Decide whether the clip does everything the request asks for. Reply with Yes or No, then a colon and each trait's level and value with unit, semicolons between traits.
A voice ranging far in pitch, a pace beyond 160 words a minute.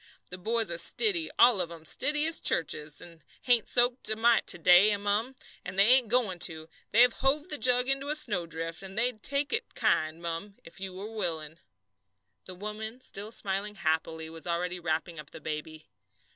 Yes: wide, 6.5 semitones; average, 185 wpm